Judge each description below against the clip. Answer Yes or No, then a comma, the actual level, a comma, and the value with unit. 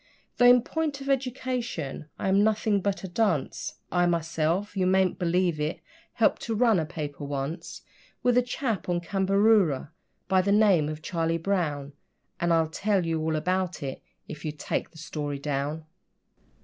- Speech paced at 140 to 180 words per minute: Yes, average, 170 wpm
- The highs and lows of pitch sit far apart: No, average, 4.9 semitones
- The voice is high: No, medium, 180 Hz